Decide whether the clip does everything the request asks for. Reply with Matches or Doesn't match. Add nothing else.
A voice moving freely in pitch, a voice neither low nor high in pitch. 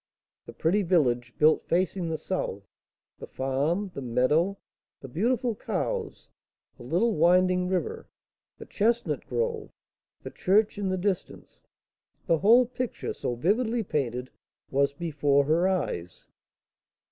Matches